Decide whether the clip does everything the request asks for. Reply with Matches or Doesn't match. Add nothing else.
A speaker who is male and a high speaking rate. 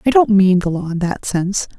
Doesn't match